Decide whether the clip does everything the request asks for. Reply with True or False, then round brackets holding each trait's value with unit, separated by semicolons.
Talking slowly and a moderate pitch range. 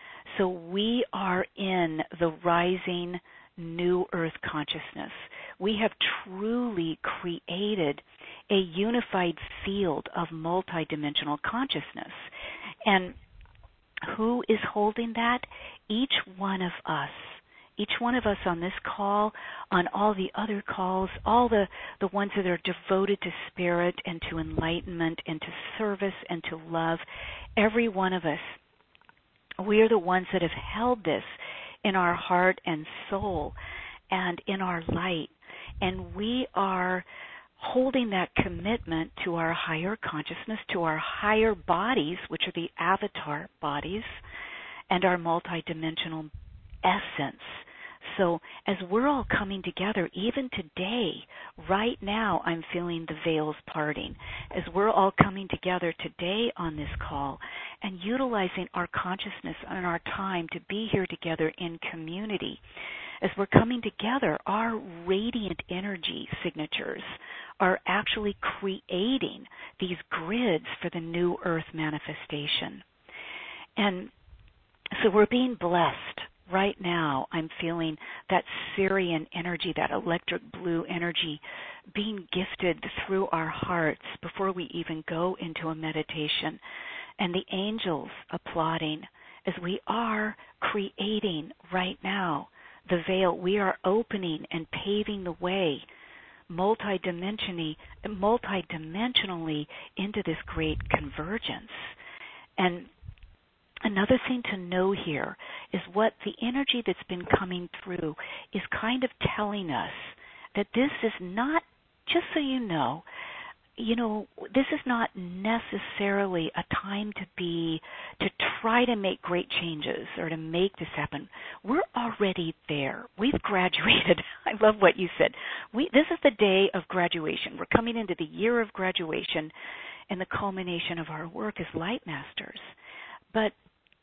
True (130 wpm; 3.9 semitones)